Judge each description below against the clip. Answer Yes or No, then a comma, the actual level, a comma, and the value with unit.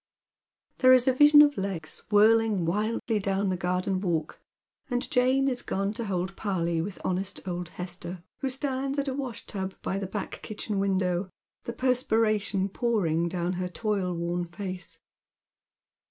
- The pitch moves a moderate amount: Yes, average, 4.7 semitones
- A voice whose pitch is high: Yes, high, 195 Hz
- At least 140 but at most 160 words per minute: Yes, average, 155 wpm